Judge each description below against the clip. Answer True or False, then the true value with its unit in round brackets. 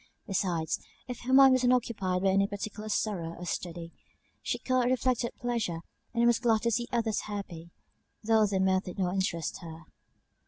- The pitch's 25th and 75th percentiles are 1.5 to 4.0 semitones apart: False (4.6 semitones)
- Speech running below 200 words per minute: True (180 wpm)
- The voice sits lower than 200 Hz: False (205 Hz)